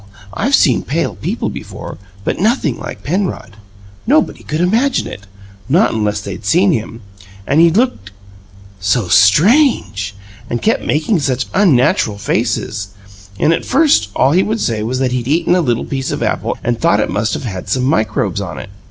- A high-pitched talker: No, low, 125 Hz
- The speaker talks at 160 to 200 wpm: Yes, average, 170 wpm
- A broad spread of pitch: Yes, wide, 9.0 semitones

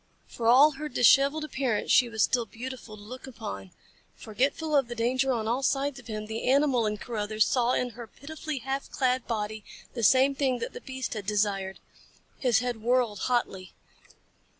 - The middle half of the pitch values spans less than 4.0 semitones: Yes, average, 3.6 semitones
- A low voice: No, high, 245 Hz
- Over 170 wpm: Yes, average, 180 wpm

